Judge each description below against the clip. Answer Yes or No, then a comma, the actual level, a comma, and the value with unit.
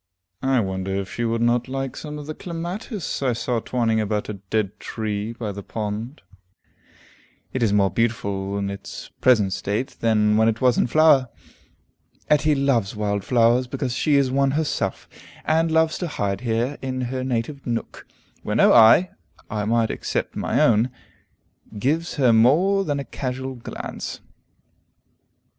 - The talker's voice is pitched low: Yes, low, 120 Hz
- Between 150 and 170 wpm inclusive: Yes, average, 160 wpm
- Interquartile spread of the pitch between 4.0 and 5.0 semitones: Yes, average, 4.4 semitones